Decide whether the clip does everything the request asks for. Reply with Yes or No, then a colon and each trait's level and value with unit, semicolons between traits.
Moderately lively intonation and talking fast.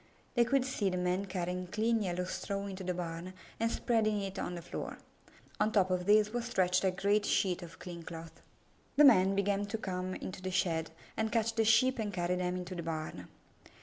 Yes: average, 3.1 semitones; fast, 215 wpm